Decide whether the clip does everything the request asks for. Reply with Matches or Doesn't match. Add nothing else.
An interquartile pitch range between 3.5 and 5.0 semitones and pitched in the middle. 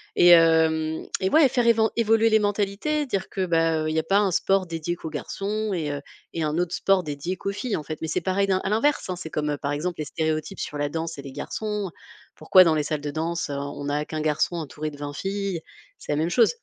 Matches